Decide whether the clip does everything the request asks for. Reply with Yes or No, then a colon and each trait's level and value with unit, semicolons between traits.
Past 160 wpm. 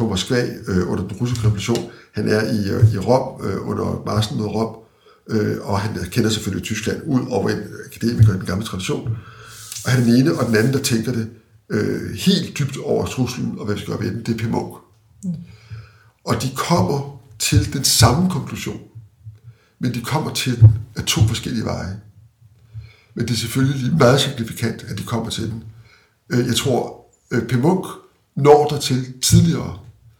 Yes: average, 180 wpm